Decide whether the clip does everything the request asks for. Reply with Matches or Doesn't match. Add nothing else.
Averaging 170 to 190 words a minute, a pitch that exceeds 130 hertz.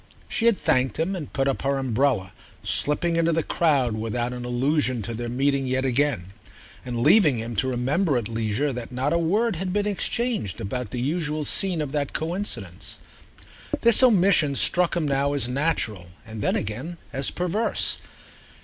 Matches